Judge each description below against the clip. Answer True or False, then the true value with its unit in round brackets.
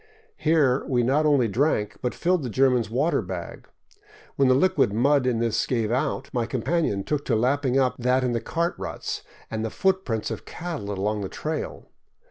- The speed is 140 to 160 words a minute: False (185 wpm)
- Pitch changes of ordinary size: True (4.5 semitones)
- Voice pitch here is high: False (130 Hz)